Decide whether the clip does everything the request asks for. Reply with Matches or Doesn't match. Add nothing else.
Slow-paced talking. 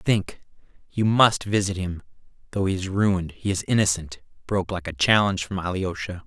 Doesn't match